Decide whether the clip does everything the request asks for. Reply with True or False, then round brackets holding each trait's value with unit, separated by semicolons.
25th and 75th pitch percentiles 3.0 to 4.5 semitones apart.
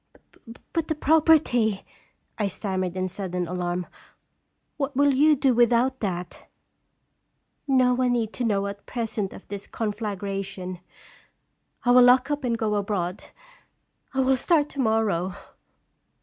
False (5.0 semitones)